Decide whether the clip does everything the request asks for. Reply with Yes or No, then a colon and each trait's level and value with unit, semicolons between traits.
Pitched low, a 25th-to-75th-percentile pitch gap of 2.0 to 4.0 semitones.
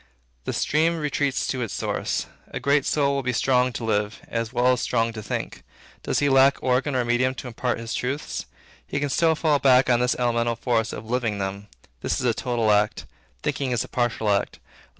Yes: low, 125 Hz; average, 3.0 semitones